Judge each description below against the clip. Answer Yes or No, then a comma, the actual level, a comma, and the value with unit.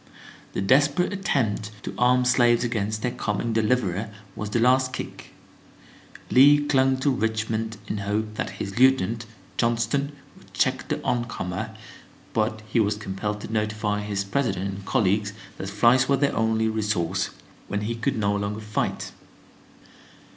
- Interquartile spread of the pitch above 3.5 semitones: No, average, 3.1 semitones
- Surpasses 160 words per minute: No, average, 150 wpm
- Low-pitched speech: Yes, low, 110 Hz